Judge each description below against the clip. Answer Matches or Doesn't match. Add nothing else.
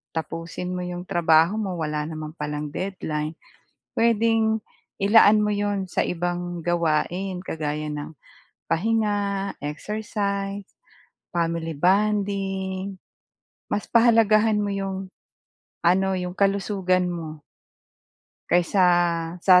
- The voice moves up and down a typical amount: Matches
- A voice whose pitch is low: Doesn't match